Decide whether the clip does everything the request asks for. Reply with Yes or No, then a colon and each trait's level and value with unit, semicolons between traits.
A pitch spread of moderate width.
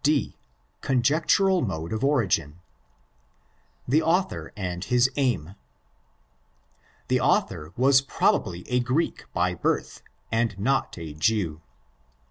No: wide, 7.8 semitones